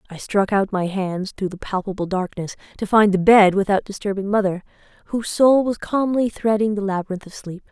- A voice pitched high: Yes, high, 200 Hz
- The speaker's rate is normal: Yes, average, 195 wpm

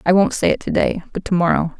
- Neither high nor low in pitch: Yes, medium, 175 Hz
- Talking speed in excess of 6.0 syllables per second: Yes, 6.4 syllables/s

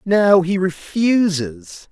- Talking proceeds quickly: No, slow, 95 wpm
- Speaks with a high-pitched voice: No, medium, 180 Hz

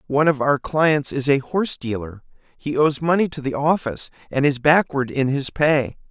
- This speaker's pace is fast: No, average, 185 wpm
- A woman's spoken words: No, male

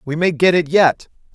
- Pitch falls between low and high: Yes, medium, 165 Hz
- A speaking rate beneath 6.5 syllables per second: Yes, 4.9 syllables/s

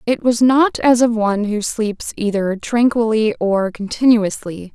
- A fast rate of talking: No, average, 150 wpm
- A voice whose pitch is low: No, high, 220 Hz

